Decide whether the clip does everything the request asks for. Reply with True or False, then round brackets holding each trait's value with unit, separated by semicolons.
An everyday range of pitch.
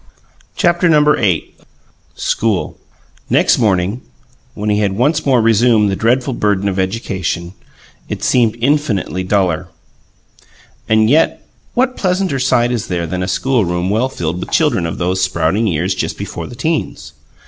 False (5.7 semitones)